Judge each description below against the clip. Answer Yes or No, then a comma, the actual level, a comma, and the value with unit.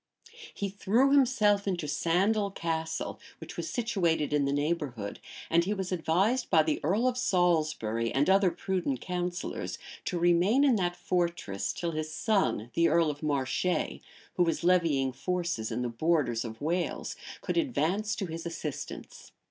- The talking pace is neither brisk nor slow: Yes, average, 155 wpm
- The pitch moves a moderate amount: Yes, average, 4.2 semitones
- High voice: No, medium, 170 Hz